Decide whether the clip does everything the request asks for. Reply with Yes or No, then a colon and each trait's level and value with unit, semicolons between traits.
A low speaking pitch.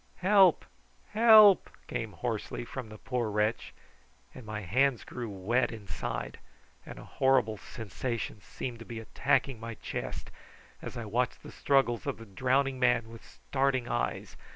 Yes: low, 120 Hz